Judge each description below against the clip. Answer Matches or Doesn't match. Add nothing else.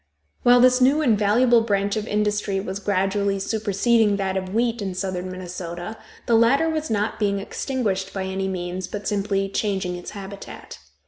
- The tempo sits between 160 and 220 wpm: Matches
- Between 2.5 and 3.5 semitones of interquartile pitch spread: Matches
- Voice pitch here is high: Matches